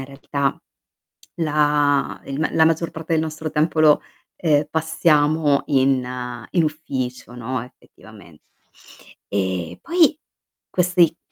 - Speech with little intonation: No, average, 3.9 semitones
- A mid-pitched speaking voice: Yes, medium, 150 Hz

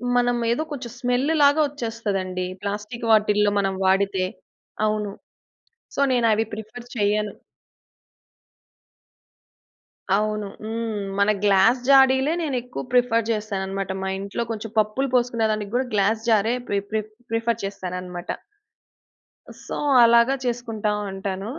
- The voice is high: Yes, high, 220 Hz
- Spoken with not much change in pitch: No, average, 3.2 semitones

